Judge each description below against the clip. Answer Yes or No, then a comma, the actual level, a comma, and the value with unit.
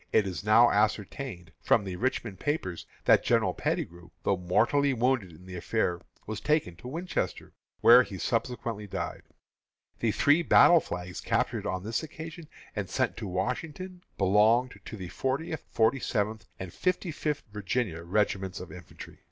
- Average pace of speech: Yes, average, 155 wpm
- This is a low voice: Yes, low, 110 Hz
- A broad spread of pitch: Yes, wide, 6.3 semitones